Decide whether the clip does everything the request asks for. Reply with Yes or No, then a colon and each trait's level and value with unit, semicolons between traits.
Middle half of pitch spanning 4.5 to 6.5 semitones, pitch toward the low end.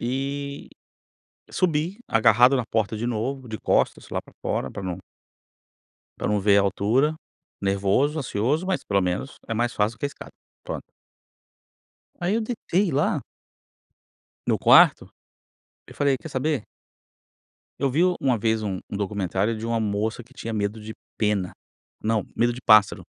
Yes: average, 5.0 semitones; low, 115 Hz